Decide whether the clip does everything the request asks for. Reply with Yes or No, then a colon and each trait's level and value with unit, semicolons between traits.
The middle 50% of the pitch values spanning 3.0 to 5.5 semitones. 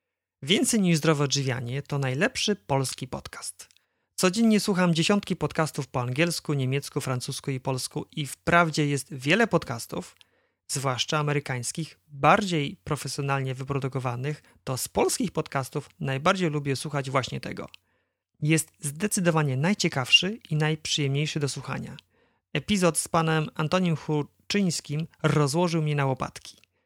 Yes: average, 3.8 semitones